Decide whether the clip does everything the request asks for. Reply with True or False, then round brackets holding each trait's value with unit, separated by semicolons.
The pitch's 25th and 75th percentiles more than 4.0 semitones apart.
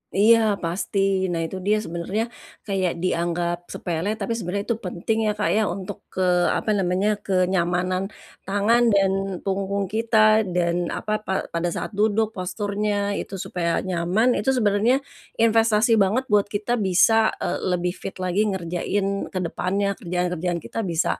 False (2.9 semitones)